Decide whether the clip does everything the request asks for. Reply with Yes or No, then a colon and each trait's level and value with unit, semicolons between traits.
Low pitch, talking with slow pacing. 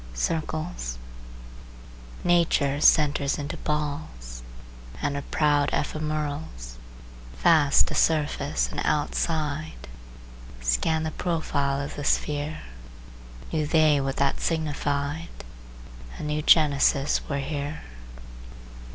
No: medium, 150 Hz; slow, 95 wpm